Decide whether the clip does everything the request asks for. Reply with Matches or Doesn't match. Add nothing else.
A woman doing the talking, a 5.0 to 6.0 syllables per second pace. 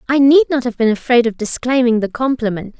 Matches